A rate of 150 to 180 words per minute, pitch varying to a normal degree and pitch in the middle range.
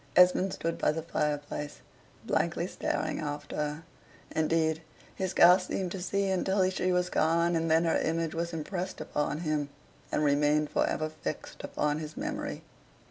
Yes: average, 160 wpm; average, 3.0 semitones; medium, 165 Hz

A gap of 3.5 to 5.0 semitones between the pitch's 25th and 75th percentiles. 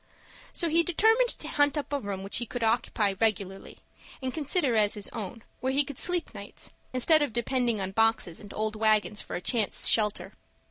No: wide, 5.4 semitones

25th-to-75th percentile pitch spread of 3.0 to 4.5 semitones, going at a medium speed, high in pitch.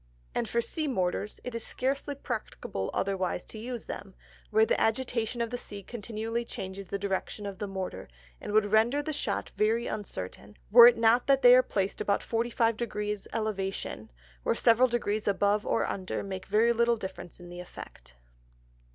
Yes: average, 3.3 semitones; average, 175 wpm; high, 215 Hz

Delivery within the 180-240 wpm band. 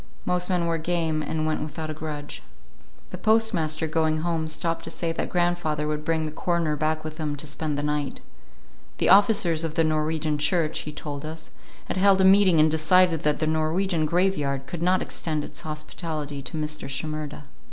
Yes: average, 190 wpm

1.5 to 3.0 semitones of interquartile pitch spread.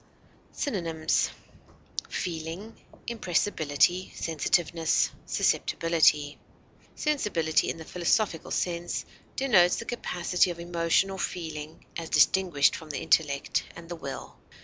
Yes: narrow, 2.5 semitones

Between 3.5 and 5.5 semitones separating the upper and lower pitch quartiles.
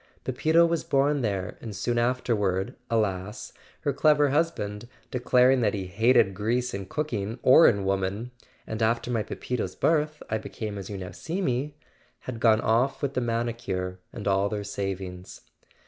Yes: average, 4.3 semitones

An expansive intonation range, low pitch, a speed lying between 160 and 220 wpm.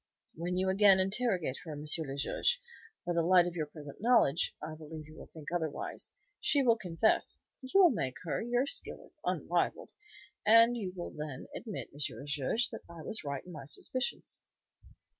No: wide, 6.7 semitones; medium, 175 Hz; average, 185 wpm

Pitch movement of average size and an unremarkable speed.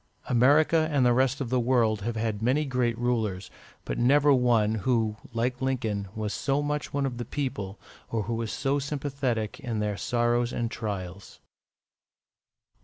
Yes: average, 3.4 semitones; average, 165 wpm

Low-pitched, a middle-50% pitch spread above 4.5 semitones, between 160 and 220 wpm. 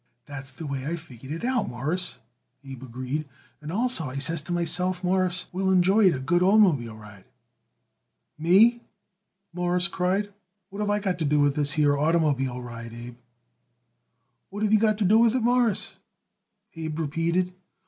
No: medium, 170 Hz; wide, 5.4 semitones; average, 170 wpm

